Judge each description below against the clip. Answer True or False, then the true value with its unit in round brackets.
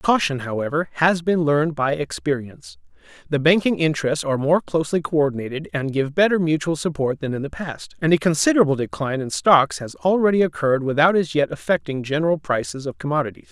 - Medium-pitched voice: True (145 Hz)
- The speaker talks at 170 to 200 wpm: True (180 wpm)